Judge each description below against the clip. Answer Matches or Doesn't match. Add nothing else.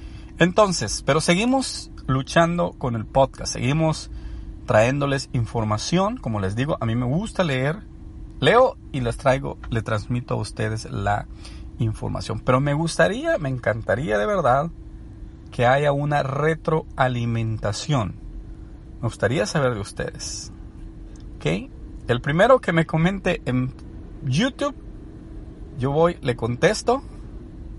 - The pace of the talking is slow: Matches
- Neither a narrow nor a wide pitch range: Doesn't match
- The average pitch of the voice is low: Matches